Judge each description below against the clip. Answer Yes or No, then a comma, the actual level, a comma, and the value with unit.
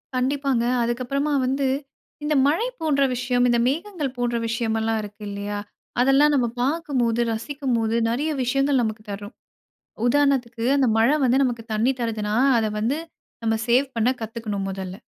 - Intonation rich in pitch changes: No, average, 3.6 semitones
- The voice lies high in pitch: Yes, high, 245 Hz